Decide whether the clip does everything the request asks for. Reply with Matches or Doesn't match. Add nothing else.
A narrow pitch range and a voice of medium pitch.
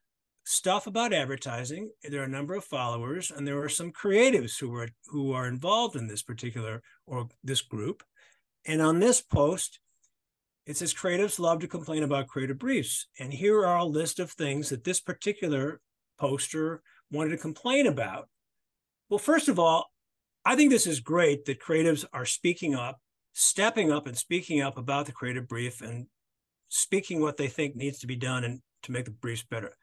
Doesn't match